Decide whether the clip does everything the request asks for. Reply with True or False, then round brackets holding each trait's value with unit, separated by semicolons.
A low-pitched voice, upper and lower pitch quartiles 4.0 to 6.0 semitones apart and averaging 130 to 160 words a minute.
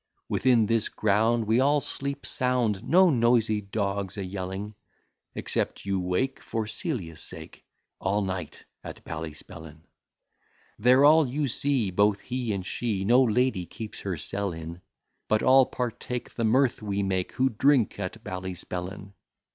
True (105 Hz; 4.8 semitones; 145 wpm)